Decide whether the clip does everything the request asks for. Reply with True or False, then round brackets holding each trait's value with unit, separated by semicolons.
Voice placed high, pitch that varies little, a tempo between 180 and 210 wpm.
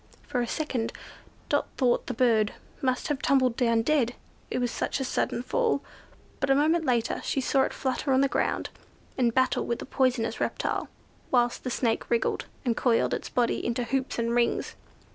True (250 Hz; 2.3 semitones; 185 wpm)